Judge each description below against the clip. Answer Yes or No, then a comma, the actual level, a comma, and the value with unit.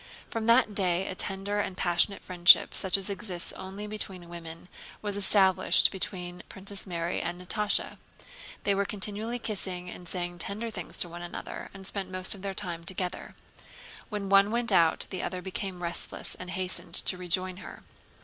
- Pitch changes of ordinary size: No, narrow, 2.2 semitones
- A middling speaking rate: Yes, average, 170 wpm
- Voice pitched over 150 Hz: Yes, high, 190 Hz